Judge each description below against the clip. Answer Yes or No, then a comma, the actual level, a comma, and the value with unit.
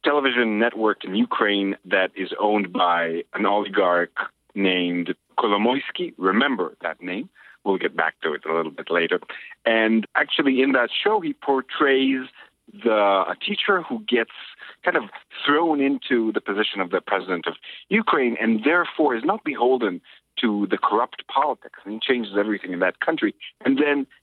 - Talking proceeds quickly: No, average, 160 wpm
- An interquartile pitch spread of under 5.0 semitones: No, wide, 5.5 semitones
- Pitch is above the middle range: No, low, 115 Hz